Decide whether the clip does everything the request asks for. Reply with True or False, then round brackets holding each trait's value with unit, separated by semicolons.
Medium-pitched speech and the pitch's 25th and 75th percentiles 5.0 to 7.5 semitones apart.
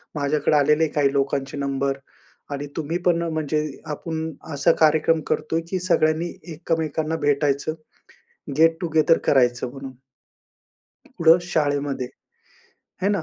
False (155 Hz; 2.4 semitones)